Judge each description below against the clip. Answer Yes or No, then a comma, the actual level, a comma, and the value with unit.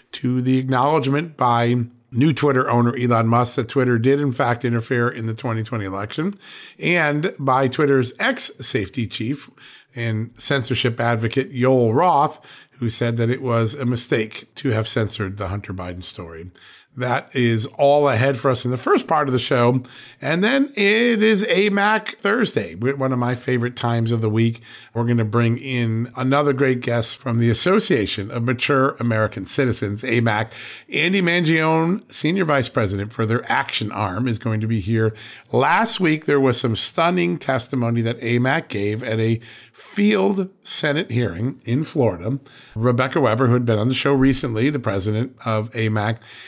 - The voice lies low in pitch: Yes, low, 125 Hz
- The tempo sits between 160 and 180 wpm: Yes, average, 170 wpm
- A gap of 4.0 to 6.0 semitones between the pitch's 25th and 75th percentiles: No, average, 3.4 semitones